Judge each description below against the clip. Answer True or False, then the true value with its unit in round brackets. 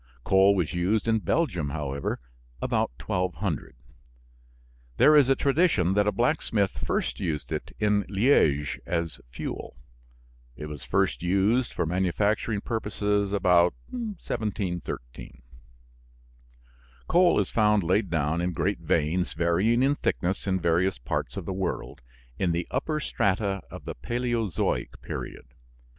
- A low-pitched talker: True (95 Hz)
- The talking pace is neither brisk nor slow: False (130 wpm)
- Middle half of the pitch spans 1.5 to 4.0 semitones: False (4.5 semitones)